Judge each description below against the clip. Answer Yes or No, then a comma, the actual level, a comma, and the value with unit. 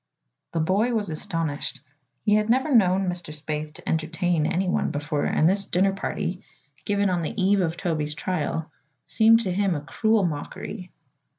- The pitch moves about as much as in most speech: Yes, average, 4.2 semitones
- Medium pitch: Yes, medium, 180 Hz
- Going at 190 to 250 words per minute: No, average, 165 wpm